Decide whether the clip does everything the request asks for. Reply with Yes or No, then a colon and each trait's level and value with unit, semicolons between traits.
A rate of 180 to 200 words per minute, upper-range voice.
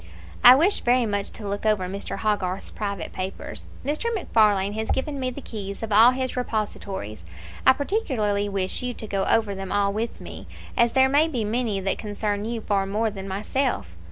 Yes: average, 190 wpm; high, 215 Hz